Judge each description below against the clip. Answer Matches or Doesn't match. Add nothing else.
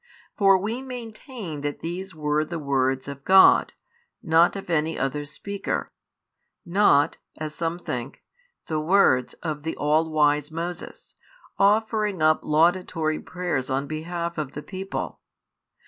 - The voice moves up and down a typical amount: Matches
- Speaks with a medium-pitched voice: Matches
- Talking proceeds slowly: Matches